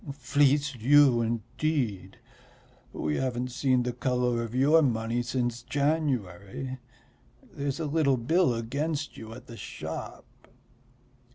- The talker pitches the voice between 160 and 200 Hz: No, low, 130 Hz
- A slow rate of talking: Yes, slow, 115 wpm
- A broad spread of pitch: No, average, 3.5 semitones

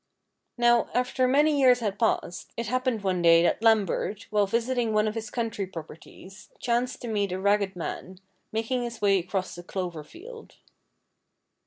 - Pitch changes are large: No, average, 4.2 semitones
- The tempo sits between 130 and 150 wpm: No, average, 165 wpm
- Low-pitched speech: No, high, 215 Hz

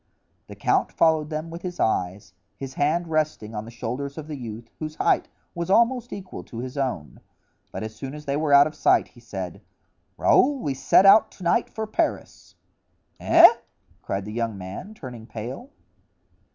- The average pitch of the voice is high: No, medium, 140 Hz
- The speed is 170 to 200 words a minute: Yes, average, 180 wpm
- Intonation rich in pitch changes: Yes, wide, 6.6 semitones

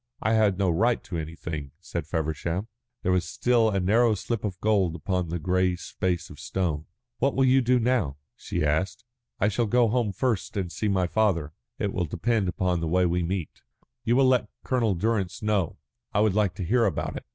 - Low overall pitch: Yes, very low, 95 Hz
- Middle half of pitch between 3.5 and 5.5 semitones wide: Yes, average, 4.3 semitones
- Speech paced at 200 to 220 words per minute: Yes, fast, 205 wpm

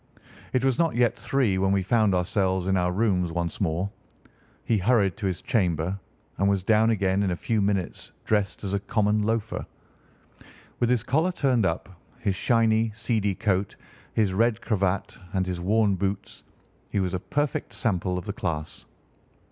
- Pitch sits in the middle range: No, low, 100 Hz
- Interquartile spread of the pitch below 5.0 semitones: Yes, average, 3.3 semitones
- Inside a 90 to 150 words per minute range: No, average, 170 wpm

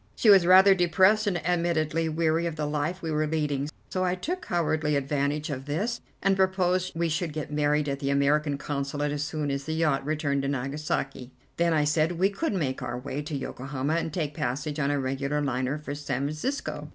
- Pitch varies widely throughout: No, average, 3.3 semitones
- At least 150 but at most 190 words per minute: No, fast, 205 wpm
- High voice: No, medium, 150 Hz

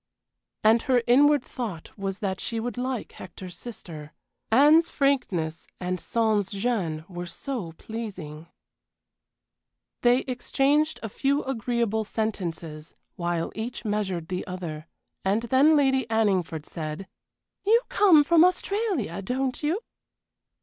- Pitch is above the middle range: Yes, high, 220 Hz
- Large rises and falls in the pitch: Yes, wide, 6.7 semitones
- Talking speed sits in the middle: No, slow, 120 wpm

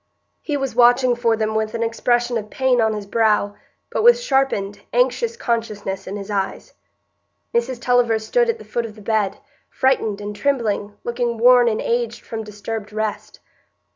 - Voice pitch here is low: No, high, 230 Hz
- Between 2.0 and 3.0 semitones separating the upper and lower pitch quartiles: Yes, narrow, 2.6 semitones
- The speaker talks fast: No, average, 170 wpm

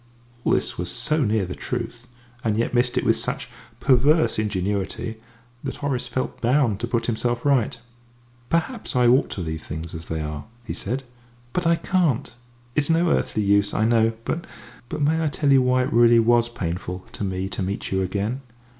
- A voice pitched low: Yes, low, 120 Hz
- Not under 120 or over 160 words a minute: No, average, 190 wpm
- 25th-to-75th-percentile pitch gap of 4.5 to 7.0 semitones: Yes, wide, 5.5 semitones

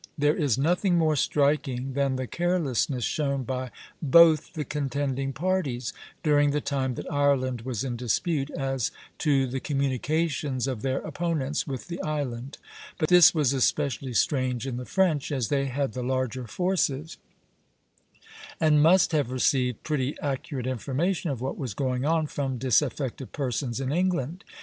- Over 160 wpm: No, average, 155 wpm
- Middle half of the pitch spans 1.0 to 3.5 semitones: Yes, average, 2.9 semitones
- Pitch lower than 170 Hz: Yes, medium, 140 Hz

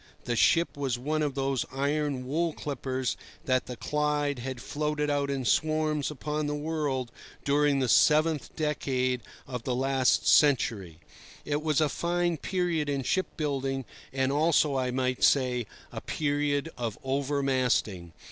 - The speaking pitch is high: No, medium, 140 Hz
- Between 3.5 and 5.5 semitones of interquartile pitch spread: No, narrow, 2.6 semitones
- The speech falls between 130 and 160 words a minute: Yes, average, 150 wpm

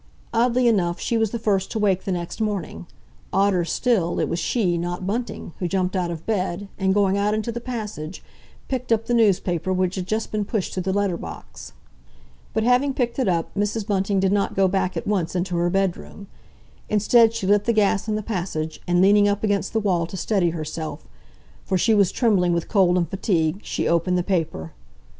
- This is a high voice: Yes, high, 195 Hz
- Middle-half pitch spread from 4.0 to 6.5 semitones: No, average, 3.4 semitones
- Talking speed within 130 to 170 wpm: No, fast, 205 wpm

